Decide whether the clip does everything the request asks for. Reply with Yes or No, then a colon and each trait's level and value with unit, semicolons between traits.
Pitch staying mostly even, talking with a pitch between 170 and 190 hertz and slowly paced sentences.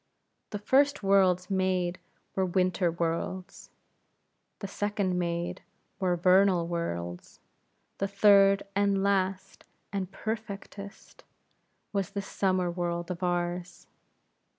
Yes: narrow, 2.1 semitones; medium, 185 Hz; slow, 105 wpm